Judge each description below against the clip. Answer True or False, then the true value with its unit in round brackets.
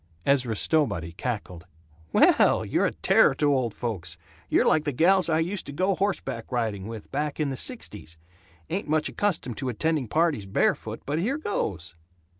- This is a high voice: False (140 Hz)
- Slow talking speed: False (170 wpm)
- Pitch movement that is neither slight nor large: False (7.3 semitones)